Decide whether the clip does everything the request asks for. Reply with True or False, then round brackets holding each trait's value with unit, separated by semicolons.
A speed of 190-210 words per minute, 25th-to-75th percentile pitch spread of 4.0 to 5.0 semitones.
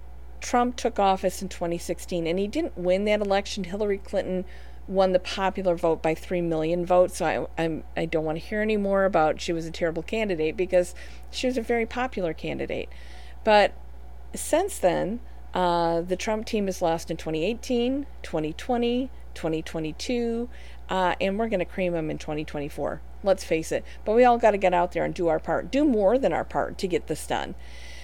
True (195 wpm; 4.6 semitones)